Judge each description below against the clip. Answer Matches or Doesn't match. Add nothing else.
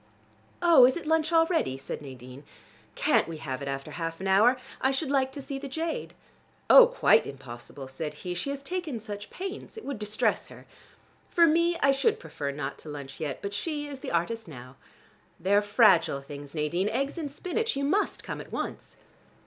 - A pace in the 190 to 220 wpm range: Matches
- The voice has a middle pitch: Doesn't match